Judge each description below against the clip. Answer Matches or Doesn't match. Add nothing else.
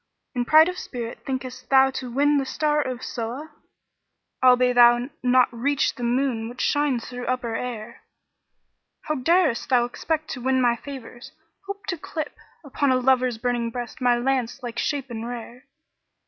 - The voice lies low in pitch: Doesn't match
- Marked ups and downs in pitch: Doesn't match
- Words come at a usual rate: Matches